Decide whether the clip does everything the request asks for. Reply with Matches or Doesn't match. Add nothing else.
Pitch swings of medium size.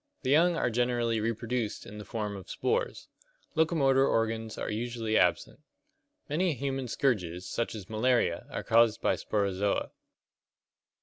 Matches